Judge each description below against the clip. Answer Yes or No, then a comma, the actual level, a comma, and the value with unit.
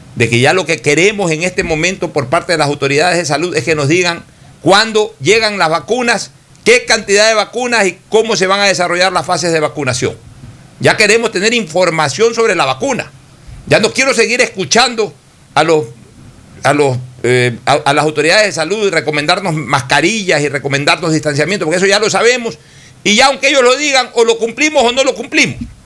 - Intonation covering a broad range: Yes, wide, 6.9 semitones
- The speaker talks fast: Yes, fast, 195 wpm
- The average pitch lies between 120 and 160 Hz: No, medium, 175 Hz